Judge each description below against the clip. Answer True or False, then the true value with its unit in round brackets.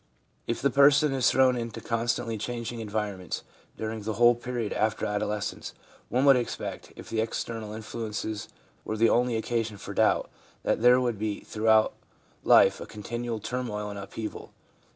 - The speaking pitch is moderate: False (115 Hz)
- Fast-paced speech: False (155 wpm)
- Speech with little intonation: True (2.1 semitones)